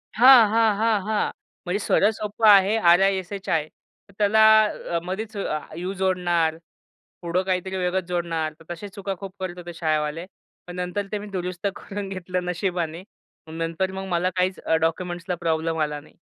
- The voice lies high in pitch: No, medium, 180 Hz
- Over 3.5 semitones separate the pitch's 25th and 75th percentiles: No, average, 2.7 semitones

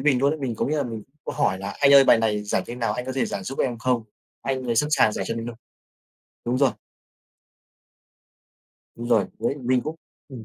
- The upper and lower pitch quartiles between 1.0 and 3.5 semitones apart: Yes, average, 3.0 semitones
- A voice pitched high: No, low, 125 Hz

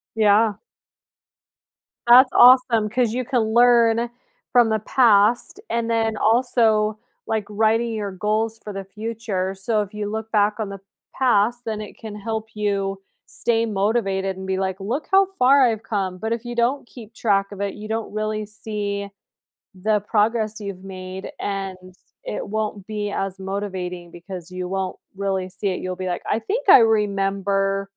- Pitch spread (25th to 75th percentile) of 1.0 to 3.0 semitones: Yes, narrow, 2.5 semitones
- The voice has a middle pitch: No, high, 210 Hz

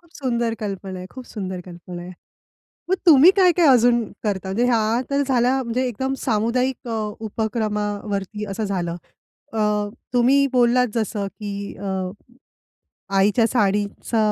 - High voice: Yes, high, 220 Hz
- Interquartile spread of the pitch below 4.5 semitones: Yes, average, 3.9 semitones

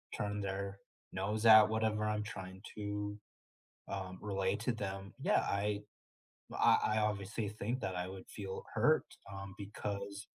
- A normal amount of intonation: No, narrow, 1.5 semitones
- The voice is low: Yes, low, 100 Hz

